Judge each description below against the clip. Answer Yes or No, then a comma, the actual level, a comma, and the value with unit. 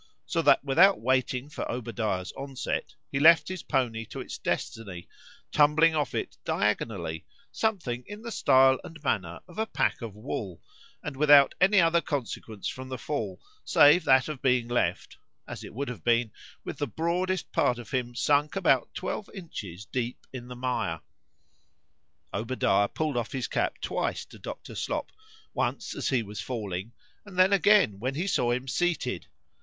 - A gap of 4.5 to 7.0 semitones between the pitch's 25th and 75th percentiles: Yes, wide, 5.5 semitones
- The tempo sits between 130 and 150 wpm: No, average, 165 wpm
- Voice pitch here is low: Yes, low, 130 Hz